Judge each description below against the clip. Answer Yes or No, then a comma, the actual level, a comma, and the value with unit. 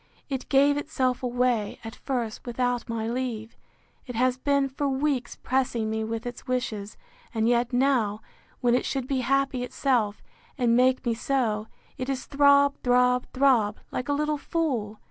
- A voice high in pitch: Yes, very high, 250 Hz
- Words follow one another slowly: No, average, 165 wpm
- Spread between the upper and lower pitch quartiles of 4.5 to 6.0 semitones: No, average, 2.8 semitones